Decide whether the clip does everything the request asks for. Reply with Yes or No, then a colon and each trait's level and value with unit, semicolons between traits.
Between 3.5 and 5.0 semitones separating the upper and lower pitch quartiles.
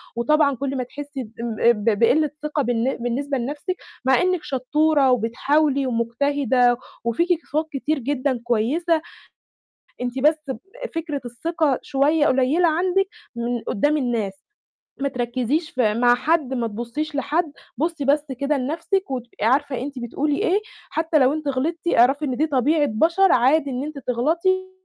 Yes: average, 4.0 semitones